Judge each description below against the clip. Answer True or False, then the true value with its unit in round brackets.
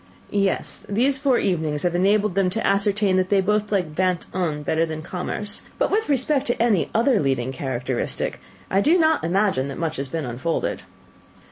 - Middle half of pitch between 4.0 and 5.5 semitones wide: True (5.0 semitones)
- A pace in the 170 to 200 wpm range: True (180 wpm)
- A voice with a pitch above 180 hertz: True (190 Hz)